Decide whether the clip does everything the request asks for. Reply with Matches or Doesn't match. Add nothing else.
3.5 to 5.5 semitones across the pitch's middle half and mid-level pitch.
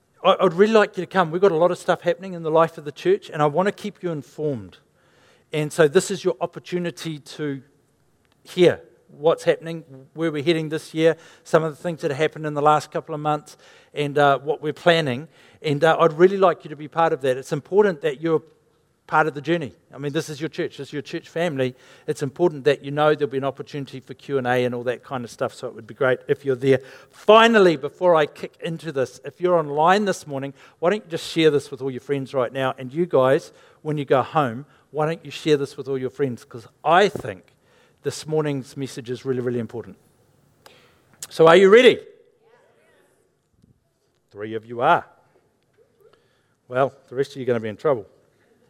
Matches